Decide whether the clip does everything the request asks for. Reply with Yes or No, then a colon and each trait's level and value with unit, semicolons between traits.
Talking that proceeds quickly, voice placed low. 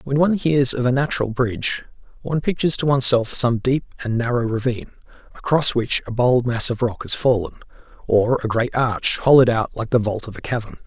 Yes: fast, 210 wpm; low, 125 Hz